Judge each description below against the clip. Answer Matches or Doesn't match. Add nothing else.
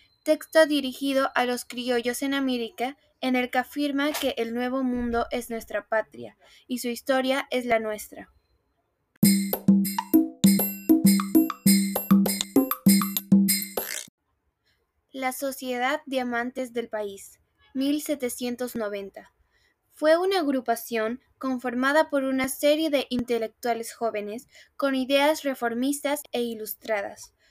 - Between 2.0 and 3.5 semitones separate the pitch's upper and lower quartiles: Doesn't match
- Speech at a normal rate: Doesn't match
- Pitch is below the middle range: Doesn't match